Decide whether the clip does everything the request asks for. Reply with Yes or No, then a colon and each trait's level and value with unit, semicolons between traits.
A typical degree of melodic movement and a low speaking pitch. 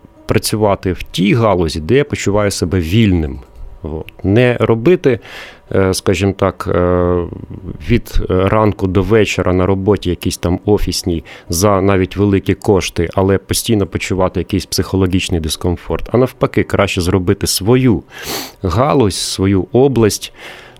Yes: average, 3.0 semitones; very low, 95 Hz